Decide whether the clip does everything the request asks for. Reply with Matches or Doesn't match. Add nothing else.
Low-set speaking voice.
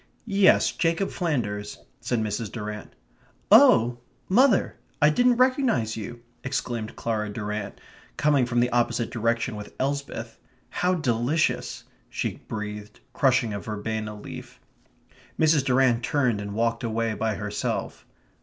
Matches